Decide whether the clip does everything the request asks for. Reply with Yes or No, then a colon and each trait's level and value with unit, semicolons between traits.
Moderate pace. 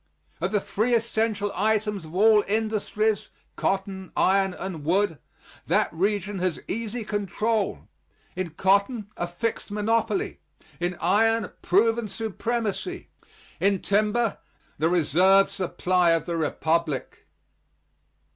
No: slow, 110 wpm